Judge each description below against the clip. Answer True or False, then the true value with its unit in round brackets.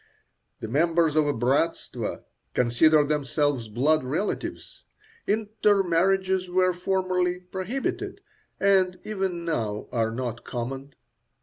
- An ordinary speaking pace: False (100 wpm)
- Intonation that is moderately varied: False (5.7 semitones)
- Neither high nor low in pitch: True (165 Hz)